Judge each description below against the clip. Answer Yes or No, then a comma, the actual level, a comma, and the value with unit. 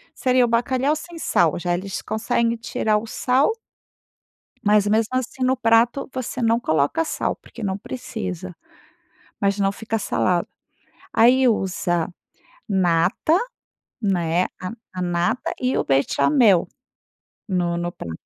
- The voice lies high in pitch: Yes, high, 215 Hz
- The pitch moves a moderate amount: No, wide, 5.9 semitones